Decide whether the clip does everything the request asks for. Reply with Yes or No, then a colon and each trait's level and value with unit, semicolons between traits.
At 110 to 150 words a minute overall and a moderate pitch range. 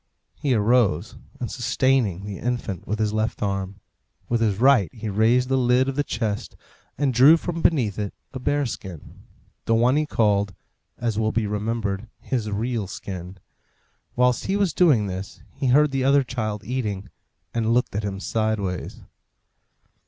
No: average, 165 wpm; average, 4.1 semitones